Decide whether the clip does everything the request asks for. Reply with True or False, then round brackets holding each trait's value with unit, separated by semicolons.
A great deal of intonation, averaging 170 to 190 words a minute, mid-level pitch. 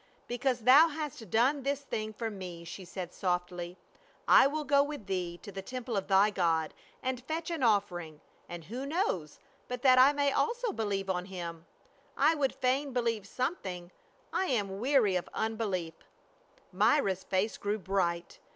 False (6.5 semitones; 175 wpm; 215 Hz)